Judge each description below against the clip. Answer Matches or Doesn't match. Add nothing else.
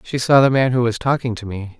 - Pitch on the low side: Matches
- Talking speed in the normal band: Doesn't match